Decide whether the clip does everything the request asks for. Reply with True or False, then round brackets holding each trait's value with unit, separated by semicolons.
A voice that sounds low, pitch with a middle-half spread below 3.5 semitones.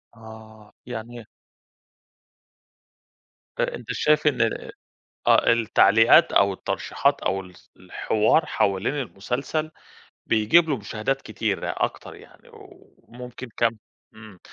True (115 Hz; 2.9 semitones)